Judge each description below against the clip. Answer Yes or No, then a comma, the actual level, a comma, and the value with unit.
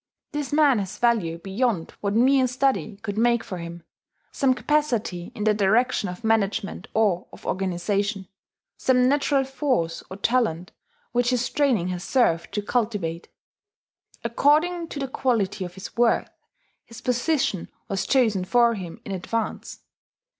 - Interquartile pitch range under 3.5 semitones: No, average, 5.1 semitones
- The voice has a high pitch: Yes, high, 225 Hz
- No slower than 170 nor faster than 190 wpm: No, average, 145 wpm